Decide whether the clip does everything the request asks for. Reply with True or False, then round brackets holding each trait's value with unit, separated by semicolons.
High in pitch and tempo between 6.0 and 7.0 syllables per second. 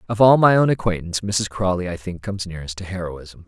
False (95 Hz; 6.4 syllables/s)